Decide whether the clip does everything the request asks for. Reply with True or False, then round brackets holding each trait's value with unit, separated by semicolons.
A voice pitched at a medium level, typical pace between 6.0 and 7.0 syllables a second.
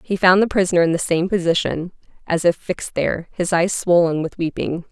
False (175 Hz; 5.7 syllables/s)